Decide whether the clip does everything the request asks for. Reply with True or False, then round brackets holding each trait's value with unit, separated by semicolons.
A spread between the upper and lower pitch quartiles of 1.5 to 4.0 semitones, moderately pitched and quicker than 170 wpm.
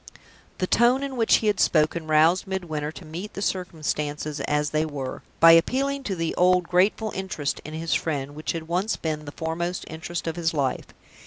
True (3.4 semitones; 165 Hz; 190 wpm)